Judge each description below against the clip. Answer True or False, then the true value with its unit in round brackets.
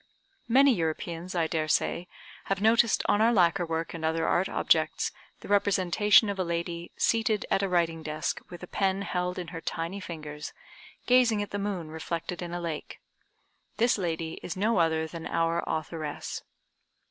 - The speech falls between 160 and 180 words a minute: True (170 wpm)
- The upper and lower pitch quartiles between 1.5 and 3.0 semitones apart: False (3.5 semitones)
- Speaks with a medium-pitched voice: True (175 Hz)